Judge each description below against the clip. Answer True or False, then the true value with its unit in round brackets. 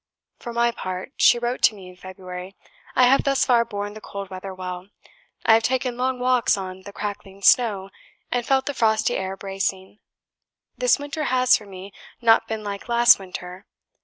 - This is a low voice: False (210 Hz)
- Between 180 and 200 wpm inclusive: True (185 wpm)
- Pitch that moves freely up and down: False (4.4 semitones)